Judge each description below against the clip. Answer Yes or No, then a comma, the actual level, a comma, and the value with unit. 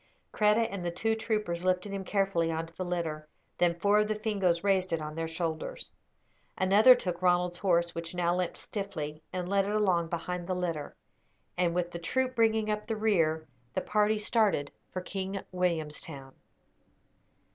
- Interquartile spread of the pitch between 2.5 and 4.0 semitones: Yes, average, 3.5 semitones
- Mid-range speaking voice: Yes, medium, 180 Hz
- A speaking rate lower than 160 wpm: No, average, 175 wpm